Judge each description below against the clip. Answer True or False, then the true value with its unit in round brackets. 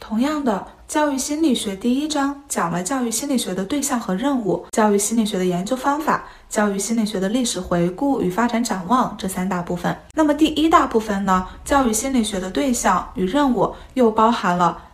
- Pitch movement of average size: False (6.5 semitones)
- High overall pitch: True (230 Hz)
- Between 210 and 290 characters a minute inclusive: False (310 characters per minute)